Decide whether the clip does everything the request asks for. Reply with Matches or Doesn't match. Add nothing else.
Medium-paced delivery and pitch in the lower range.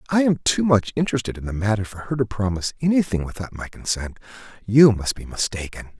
Matches